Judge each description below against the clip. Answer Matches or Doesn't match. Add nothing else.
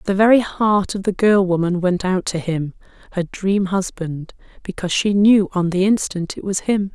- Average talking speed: Matches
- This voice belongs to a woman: Matches